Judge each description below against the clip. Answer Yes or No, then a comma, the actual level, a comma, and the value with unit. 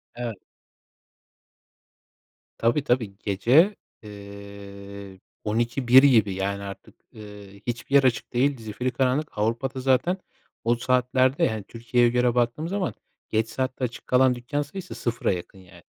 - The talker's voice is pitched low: Yes, low, 120 Hz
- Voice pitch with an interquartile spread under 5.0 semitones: Yes, average, 4.0 semitones